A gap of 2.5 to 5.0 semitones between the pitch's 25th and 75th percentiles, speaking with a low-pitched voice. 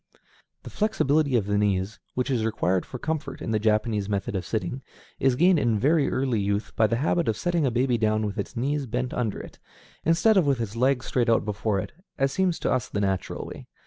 Yes: average, 4.6 semitones; low, 120 Hz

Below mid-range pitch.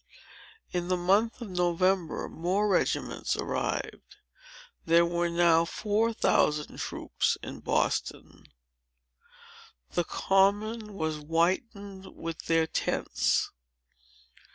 No: medium, 180 Hz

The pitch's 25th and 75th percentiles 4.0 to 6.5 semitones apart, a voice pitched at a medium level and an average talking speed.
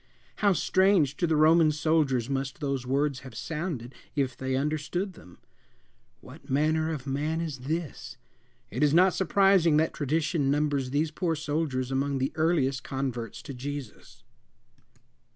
No: average, 3.2 semitones; medium, 150 Hz; average, 145 wpm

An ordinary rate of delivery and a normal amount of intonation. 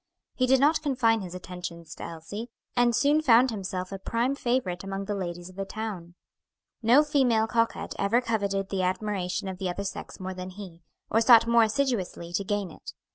Yes: average, 190 wpm; average, 4.3 semitones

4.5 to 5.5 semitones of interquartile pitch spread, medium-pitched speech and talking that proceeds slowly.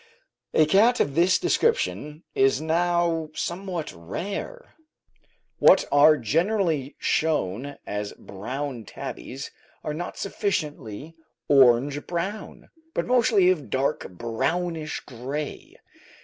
Yes: average, 4.9 semitones; medium, 155 Hz; slow, 105 wpm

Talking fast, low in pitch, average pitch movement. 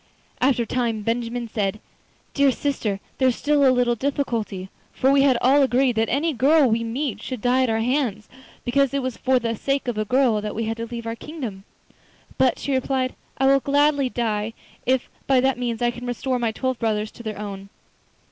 No: fast, 210 wpm; high, 245 Hz; average, 3.0 semitones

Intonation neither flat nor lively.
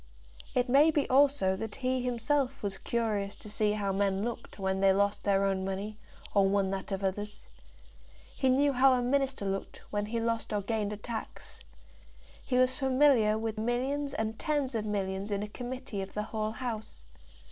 Yes: average, 4.2 semitones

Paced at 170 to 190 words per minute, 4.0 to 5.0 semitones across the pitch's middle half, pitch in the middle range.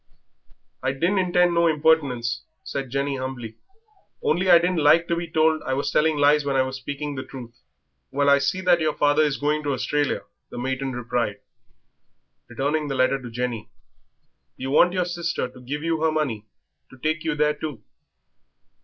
No: average, 180 wpm; average, 3.4 semitones; medium, 145 Hz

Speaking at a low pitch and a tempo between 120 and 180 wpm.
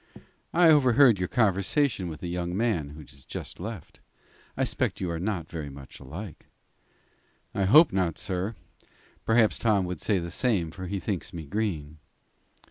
Yes: very low, 95 Hz; average, 170 wpm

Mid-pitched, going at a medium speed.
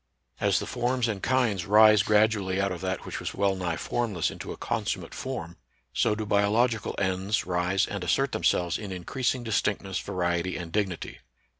No: low, 100 Hz; average, 175 wpm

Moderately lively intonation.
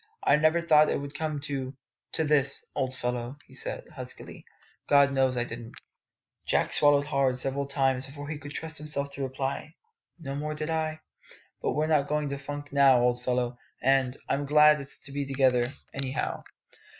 No: narrow, 2.3 semitones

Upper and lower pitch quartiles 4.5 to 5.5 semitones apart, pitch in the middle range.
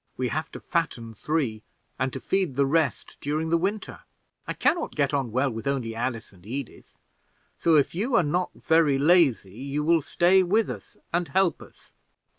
Yes: average, 4.8 semitones; medium, 150 Hz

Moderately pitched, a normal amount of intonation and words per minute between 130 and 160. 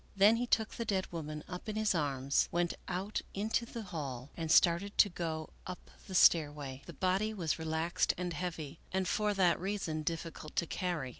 No: medium, 175 Hz; average, 3.9 semitones; average, 195 wpm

